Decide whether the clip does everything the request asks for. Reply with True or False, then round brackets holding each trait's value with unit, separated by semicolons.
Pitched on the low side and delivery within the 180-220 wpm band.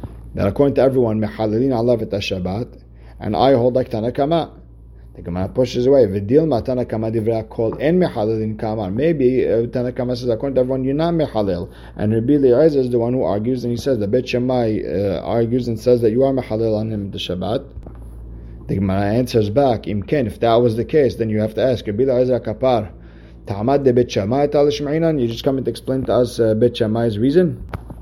True (120 Hz; 190 wpm)